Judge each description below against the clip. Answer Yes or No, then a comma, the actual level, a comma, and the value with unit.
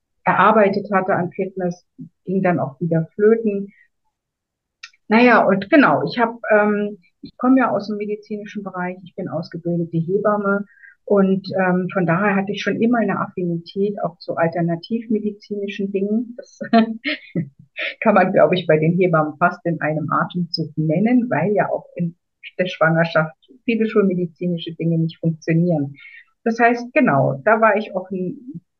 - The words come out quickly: No, average, 150 wpm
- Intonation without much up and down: No, average, 3.8 semitones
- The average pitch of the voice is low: No, high, 195 Hz